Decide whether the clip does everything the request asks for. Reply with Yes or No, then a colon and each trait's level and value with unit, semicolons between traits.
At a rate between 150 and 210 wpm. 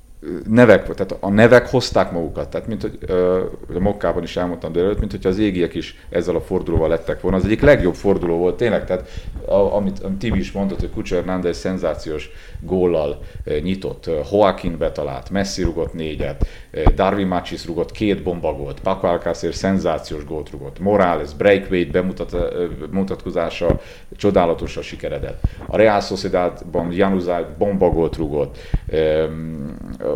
Yes: fast, 155 wpm